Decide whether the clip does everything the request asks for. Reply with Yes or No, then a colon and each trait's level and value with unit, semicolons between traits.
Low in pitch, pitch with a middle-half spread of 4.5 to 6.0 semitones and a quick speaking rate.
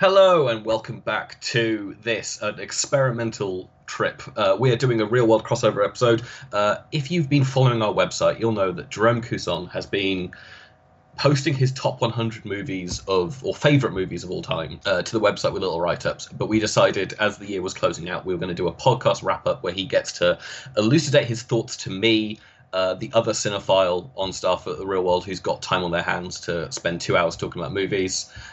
Yes: low, 110 Hz; average, 5.0 semitones; fast, 210 wpm